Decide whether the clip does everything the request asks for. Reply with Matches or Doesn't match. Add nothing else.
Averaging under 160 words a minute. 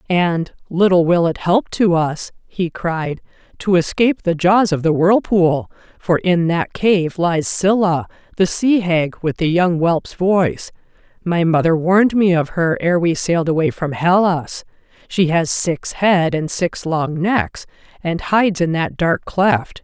Doesn't match